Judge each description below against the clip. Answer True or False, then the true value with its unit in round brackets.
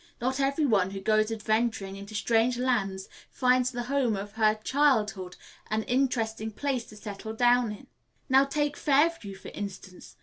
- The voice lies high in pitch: True (225 Hz)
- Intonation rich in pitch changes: False (3.8 semitones)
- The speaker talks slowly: False (165 wpm)